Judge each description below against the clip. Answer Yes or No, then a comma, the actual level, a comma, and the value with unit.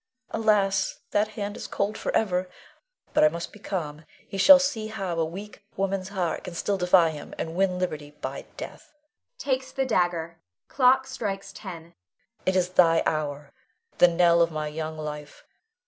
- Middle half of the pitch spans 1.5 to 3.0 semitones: No, average, 4.0 semitones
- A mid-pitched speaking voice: Yes, medium, 180 Hz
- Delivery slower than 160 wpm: No, average, 165 wpm